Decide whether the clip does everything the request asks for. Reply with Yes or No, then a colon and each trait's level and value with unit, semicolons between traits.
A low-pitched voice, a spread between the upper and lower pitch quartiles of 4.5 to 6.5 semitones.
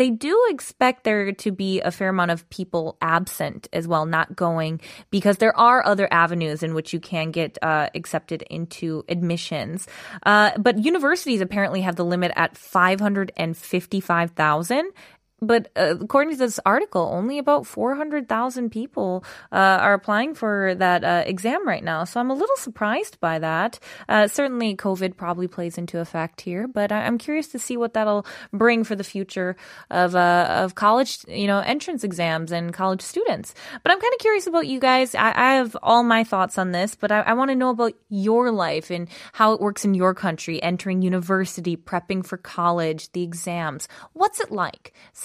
No: high, 195 Hz; average, 5.2 semitones